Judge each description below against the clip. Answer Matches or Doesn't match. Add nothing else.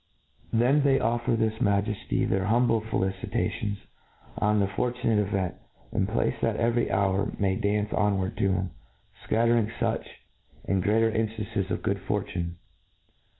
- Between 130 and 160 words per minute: Matches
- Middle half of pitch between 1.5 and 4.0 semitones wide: Matches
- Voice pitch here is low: Matches